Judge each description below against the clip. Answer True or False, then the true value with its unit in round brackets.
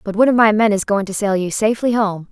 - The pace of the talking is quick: True (310 wpm)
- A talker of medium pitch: False (210 Hz)